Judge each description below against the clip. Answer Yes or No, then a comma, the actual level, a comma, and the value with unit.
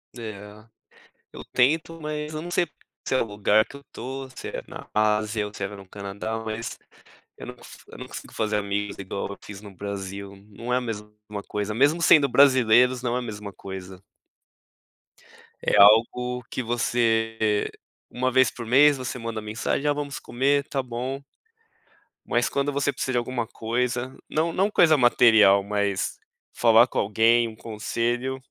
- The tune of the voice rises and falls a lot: No, average, 3.9 semitones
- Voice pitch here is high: No, low, 115 Hz